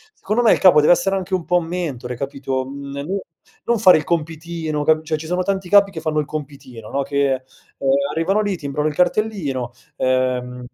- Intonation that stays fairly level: No, average, 4.7 semitones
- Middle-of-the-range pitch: Yes, medium, 155 Hz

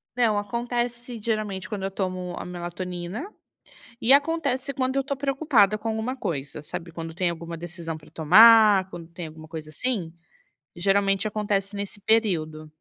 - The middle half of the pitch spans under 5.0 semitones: No, average, 5.3 semitones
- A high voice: Yes, high, 200 Hz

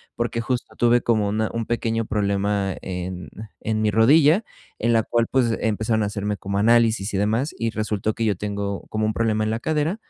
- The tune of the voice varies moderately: No, narrow, 2.2 semitones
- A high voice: No, low, 110 Hz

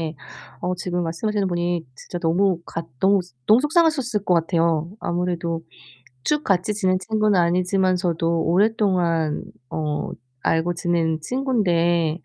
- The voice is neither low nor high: Yes, medium, 175 Hz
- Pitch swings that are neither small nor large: Yes, average, 3.2 semitones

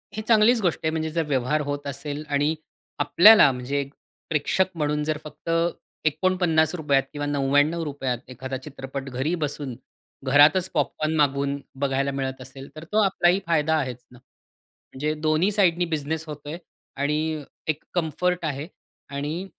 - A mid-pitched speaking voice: Yes, medium, 150 Hz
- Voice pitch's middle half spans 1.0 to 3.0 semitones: Yes, narrow, 2.6 semitones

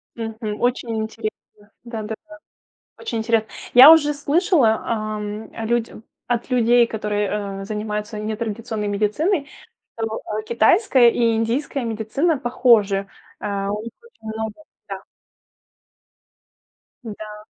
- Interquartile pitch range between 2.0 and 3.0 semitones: Yes, narrow, 2.4 semitones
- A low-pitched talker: No, high, 225 Hz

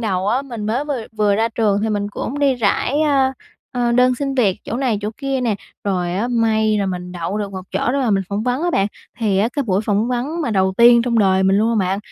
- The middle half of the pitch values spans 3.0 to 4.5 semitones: Yes, average, 3.9 semitones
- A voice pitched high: Yes, high, 225 Hz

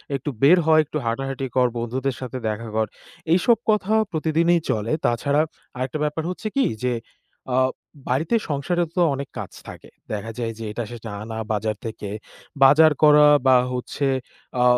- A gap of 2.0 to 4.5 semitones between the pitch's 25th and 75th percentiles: No, average, 5.2 semitones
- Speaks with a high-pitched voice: No, low, 135 Hz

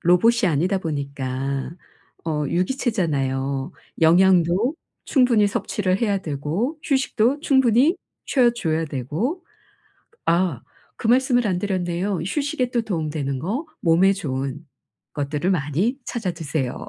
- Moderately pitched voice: Yes, medium, 180 Hz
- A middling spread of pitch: No, wide, 7.9 semitones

